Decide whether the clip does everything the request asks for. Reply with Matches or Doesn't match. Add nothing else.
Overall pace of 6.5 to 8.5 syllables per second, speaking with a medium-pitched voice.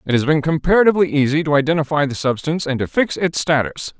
Matches